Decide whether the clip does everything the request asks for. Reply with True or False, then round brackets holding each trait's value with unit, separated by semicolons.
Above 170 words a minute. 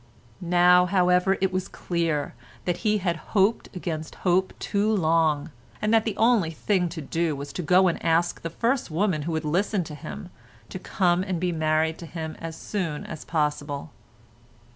True (180 wpm)